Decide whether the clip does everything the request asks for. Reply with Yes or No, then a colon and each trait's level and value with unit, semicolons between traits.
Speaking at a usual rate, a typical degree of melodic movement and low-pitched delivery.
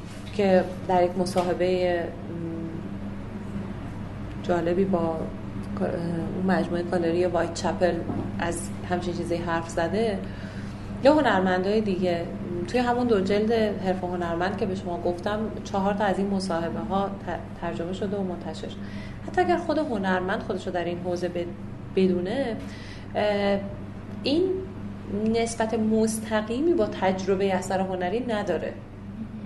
No: average, 115 wpm; average, 3.4 semitones; medium, 180 Hz